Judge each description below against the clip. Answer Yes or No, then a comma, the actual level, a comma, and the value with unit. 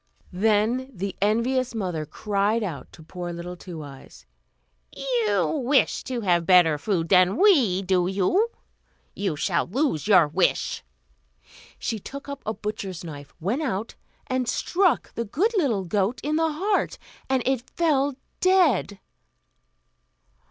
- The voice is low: No, high, 210 Hz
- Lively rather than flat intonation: Yes, wide, 6.7 semitones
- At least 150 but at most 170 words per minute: No, average, 140 wpm